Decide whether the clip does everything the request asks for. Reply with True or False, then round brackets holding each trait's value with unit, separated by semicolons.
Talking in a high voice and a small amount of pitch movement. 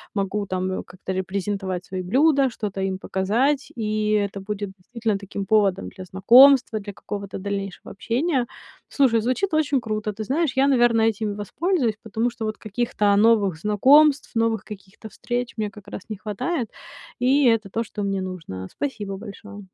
False (210 Hz; 3.6 semitones)